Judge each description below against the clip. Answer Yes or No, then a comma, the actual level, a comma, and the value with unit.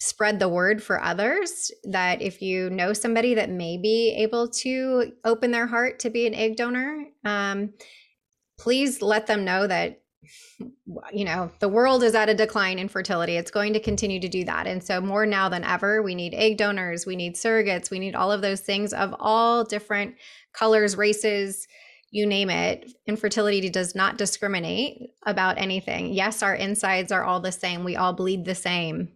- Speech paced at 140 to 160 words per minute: No, average, 185 wpm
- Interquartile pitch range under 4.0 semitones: Yes, average, 2.9 semitones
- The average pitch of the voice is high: Yes, high, 205 Hz